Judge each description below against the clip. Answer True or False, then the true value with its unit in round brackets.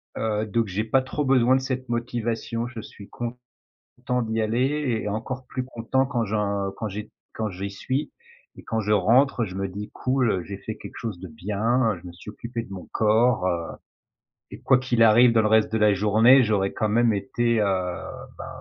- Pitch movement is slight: False (3.3 semitones)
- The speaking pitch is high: False (110 Hz)